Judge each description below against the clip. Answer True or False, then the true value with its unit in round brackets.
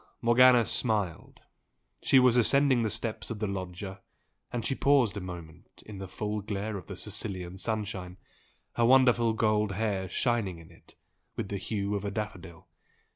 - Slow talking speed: False (165 wpm)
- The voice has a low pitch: True (105 Hz)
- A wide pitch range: False (3.4 semitones)